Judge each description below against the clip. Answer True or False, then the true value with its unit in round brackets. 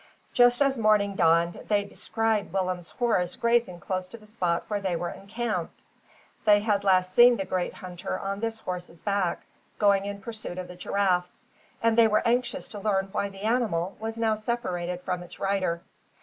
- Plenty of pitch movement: False (3.4 semitones)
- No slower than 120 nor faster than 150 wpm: False (180 wpm)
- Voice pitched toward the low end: False (200 Hz)